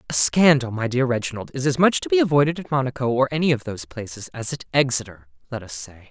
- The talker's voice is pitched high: No, low, 125 Hz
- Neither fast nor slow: No, fast, 235 wpm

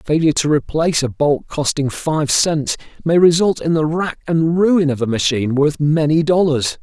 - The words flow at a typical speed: Yes, average, 185 wpm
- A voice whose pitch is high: No, medium, 155 Hz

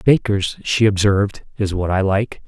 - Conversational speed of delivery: Yes, average, 170 wpm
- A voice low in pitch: Yes, low, 100 Hz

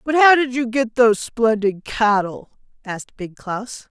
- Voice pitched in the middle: No, high, 230 Hz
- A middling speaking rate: Yes, average, 165 wpm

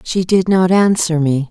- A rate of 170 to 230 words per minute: Yes, average, 200 wpm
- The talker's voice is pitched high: No, medium, 175 Hz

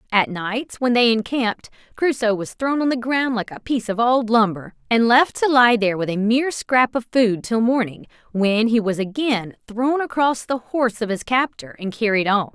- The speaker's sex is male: No, female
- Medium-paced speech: No, fast, 210 wpm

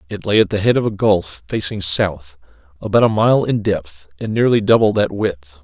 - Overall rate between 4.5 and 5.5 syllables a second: Yes, 5.0 syllables/s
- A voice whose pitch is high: No, very low, 95 Hz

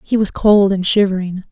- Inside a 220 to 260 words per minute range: No, average, 200 wpm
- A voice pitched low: No, high, 195 Hz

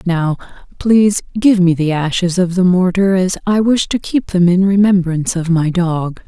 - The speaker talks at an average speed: Yes, average, 190 wpm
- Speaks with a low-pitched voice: No, medium, 185 Hz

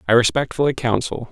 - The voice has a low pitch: Yes, low, 125 Hz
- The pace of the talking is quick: No, slow, 135 wpm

